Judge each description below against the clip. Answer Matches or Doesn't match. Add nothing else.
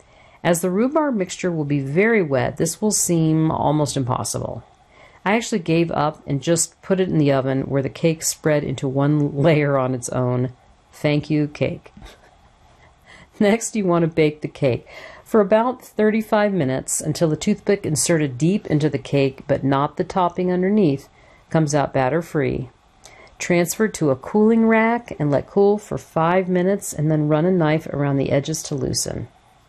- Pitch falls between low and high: Matches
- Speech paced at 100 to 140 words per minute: Doesn't match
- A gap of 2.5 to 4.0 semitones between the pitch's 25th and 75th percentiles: Doesn't match